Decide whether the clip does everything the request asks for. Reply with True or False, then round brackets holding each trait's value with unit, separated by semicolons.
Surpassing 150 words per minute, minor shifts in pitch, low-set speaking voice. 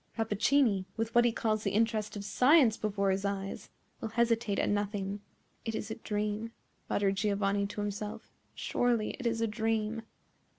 False (165 wpm; 2.0 semitones; 215 Hz)